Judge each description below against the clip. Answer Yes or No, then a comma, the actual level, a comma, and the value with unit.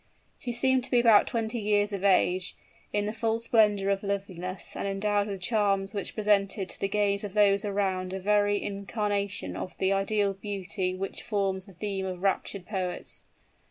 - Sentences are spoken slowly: No, average, 180 wpm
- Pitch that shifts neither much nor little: No, narrow, 1.4 semitones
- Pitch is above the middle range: Yes, high, 200 Hz